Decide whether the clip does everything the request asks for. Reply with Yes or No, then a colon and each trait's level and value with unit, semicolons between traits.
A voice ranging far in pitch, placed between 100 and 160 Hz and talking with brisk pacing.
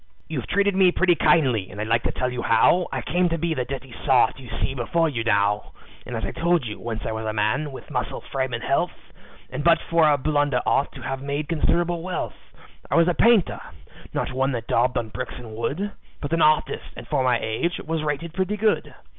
Yes: wide, 5.8 semitones; medium, 140 Hz; fast, 225 wpm